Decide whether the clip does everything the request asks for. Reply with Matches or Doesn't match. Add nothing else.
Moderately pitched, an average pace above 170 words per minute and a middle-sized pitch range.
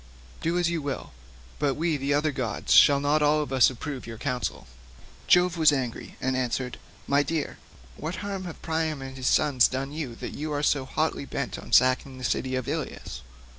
Matches